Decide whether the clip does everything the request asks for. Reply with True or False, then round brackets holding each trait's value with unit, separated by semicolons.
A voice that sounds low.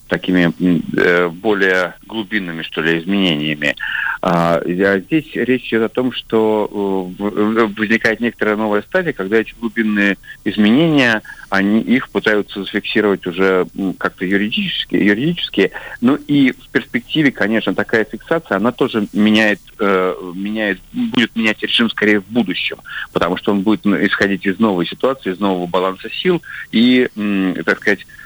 True (105 Hz)